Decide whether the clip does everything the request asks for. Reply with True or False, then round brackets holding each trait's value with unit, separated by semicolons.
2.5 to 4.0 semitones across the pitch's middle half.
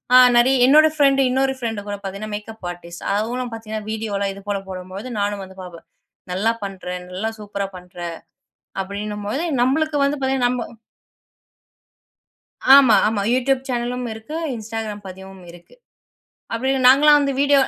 False (4.6 semitones)